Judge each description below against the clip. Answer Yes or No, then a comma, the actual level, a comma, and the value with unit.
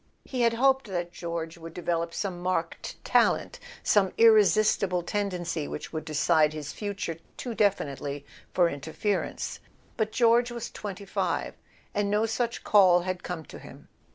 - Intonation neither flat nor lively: Yes, average, 4.3 semitones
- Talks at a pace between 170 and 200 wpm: No, average, 150 wpm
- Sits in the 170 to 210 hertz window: Yes, medium, 185 Hz